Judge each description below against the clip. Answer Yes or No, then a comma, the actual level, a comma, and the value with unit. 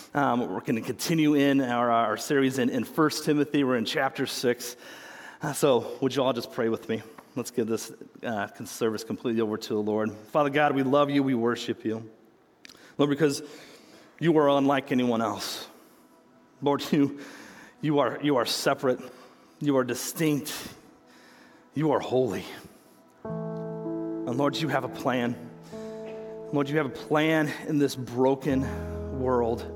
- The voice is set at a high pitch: No, low, 135 Hz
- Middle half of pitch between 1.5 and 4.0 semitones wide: Yes, average, 3.7 semitones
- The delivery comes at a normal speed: Yes, average, 155 wpm